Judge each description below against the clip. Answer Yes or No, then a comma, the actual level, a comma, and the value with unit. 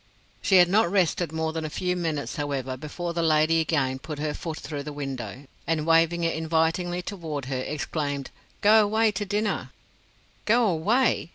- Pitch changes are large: No, average, 3.4 semitones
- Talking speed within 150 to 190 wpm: Yes, average, 175 wpm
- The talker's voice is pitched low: No, medium, 160 Hz